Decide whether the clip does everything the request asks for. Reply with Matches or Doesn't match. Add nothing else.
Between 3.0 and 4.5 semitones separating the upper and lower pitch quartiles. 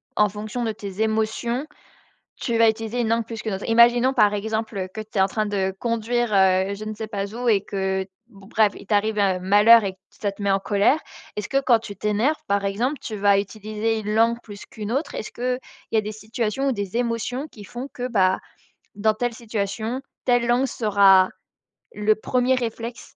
Doesn't match